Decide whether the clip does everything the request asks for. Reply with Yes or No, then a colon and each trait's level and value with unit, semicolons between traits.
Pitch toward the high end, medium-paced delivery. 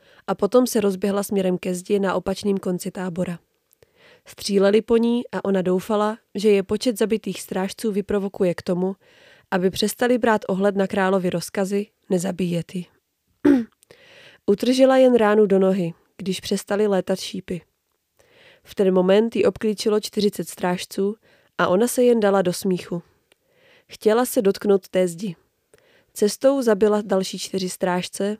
Yes: high, 200 Hz; average, 140 wpm